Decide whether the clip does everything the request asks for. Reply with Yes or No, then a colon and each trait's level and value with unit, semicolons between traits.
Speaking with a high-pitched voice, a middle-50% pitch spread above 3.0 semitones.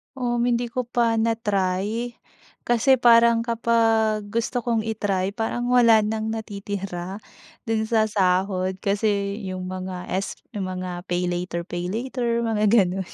Yes: high, 215 Hz; average, 3.6 semitones